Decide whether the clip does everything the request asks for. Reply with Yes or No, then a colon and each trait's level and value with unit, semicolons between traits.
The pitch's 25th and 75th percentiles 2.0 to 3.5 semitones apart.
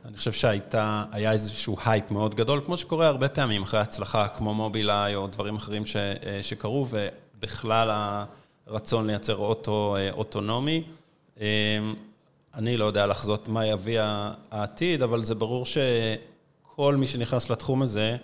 Yes: average, 3.0 semitones